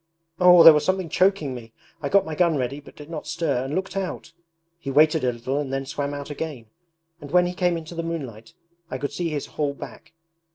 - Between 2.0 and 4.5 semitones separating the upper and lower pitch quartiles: Yes, average, 3.6 semitones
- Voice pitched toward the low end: No, medium, 150 Hz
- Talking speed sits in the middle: No, fast, 230 wpm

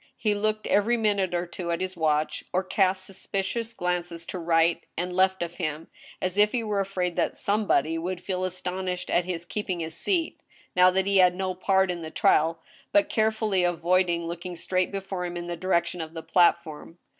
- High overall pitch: No, medium, 180 Hz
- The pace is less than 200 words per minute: No, fast, 205 wpm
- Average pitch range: No, narrow, 2.1 semitones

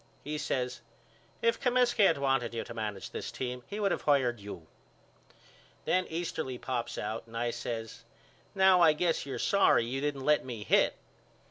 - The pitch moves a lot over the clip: Yes, wide, 6.2 semitones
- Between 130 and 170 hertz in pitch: Yes, low, 135 Hz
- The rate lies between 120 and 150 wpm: No, average, 170 wpm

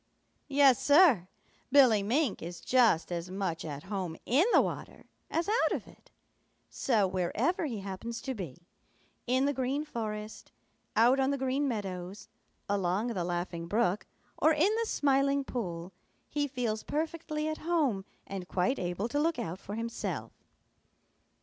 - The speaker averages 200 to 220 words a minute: No, average, 150 wpm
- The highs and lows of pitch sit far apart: Yes, wide, 7.0 semitones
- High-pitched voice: Yes, high, 230 Hz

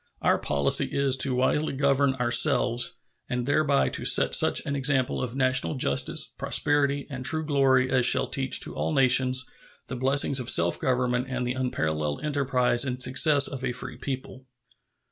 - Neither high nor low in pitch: No, low, 130 Hz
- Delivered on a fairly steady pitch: Yes, narrow, 1.9 semitones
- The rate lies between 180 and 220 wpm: No, average, 165 wpm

